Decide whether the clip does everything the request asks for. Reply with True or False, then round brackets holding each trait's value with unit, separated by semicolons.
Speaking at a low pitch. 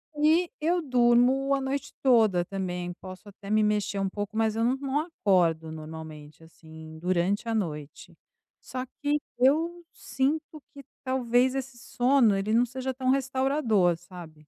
False (230 Hz)